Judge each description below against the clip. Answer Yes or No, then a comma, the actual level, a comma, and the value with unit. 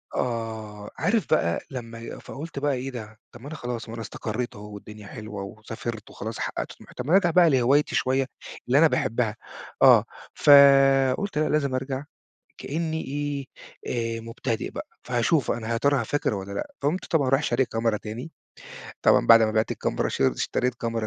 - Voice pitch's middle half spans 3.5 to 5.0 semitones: Yes, average, 4.1 semitones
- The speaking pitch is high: No, low, 125 Hz